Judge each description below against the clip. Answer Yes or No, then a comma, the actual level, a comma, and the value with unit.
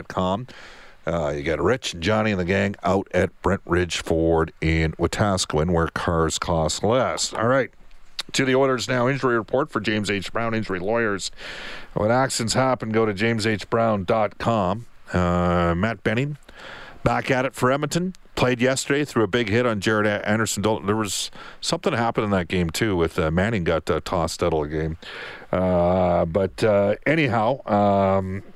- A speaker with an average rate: Yes, average, 170 wpm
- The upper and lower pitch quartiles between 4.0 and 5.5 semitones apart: Yes, average, 4.6 semitones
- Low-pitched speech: Yes, low, 105 Hz